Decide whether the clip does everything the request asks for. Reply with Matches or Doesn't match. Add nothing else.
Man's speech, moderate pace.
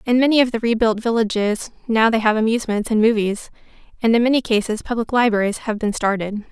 Doesn't match